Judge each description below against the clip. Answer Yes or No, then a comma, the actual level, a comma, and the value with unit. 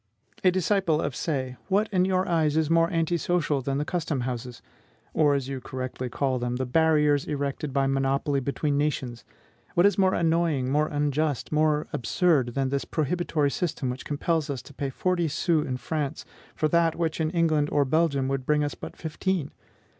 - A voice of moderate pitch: Yes, medium, 150 Hz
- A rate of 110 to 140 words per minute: No, average, 190 wpm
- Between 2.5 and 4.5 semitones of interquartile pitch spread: Yes, average, 3.4 semitones